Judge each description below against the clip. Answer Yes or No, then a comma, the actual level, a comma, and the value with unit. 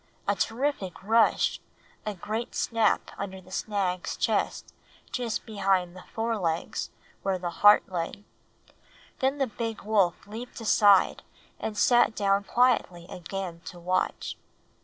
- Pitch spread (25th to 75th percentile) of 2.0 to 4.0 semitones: Yes, average, 3.4 semitones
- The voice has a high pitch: Yes, high, 205 Hz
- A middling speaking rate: No, slow, 130 wpm